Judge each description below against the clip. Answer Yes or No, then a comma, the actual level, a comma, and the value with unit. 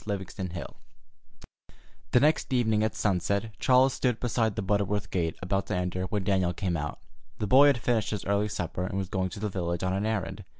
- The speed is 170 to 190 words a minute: No, fast, 205 wpm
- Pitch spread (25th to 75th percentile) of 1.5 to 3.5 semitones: Yes, average, 3.2 semitones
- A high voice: No, low, 100 Hz